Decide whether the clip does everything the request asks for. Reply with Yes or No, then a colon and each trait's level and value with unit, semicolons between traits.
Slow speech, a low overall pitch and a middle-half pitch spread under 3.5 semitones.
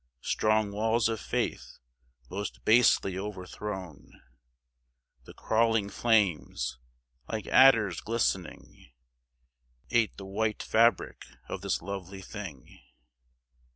Yes: slow, 90 wpm; low, 105 Hz; average, 2.8 semitones